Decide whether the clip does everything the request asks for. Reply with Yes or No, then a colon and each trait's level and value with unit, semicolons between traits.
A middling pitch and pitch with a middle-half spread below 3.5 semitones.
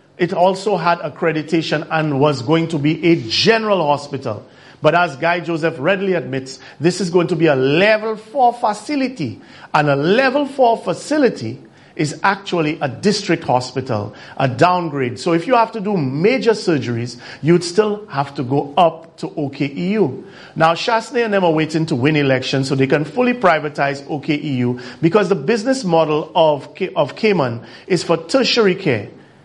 No: medium, 165 Hz; wide, 5.6 semitones